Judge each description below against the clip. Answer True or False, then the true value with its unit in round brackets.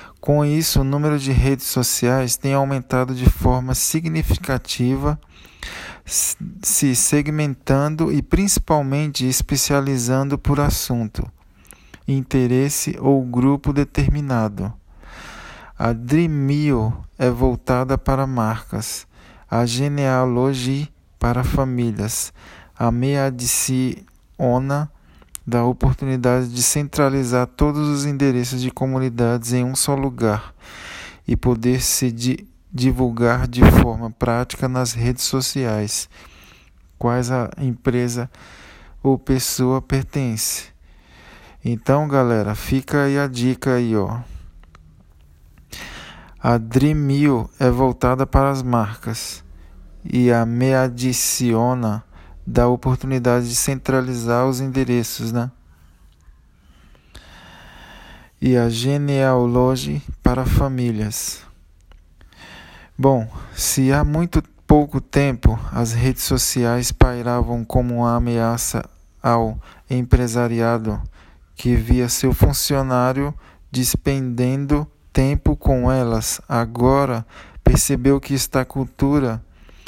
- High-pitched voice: False (125 Hz)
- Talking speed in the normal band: False (95 wpm)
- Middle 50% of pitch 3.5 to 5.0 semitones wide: False (2.8 semitones)